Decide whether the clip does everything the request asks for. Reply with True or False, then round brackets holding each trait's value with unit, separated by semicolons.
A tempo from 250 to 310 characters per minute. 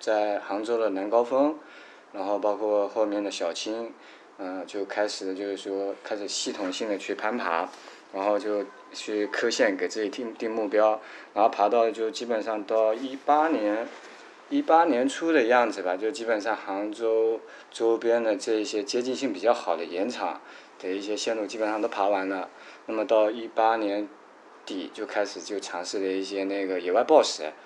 True (265 characters per minute)